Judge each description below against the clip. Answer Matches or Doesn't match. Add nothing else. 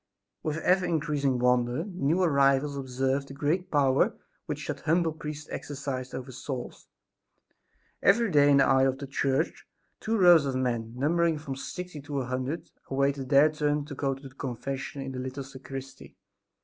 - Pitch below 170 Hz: Matches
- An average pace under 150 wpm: Doesn't match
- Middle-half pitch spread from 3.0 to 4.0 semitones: Doesn't match